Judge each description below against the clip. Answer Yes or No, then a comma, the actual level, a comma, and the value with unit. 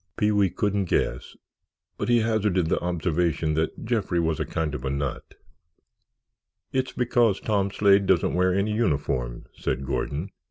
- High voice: No, very low, 90 Hz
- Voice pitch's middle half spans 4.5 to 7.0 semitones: Yes, average, 5.2 semitones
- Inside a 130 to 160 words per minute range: Yes, average, 155 wpm